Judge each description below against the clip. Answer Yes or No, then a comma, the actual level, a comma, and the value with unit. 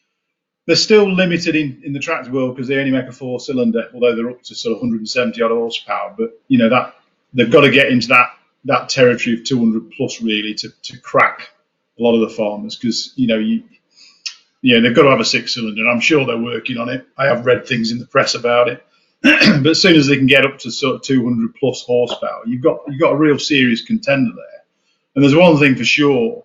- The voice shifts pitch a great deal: Yes, wide, 5.9 semitones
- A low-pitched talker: Yes, low, 130 Hz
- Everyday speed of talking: No, fast, 235 wpm